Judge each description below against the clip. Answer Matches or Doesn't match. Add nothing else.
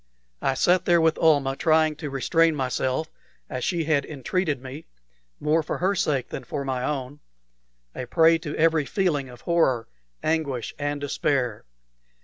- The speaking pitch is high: Doesn't match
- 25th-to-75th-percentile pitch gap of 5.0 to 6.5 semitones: Doesn't match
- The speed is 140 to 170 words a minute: Matches